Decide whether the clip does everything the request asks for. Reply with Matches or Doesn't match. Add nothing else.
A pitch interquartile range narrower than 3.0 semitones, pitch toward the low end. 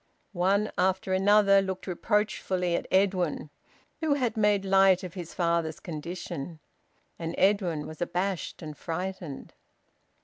Doesn't match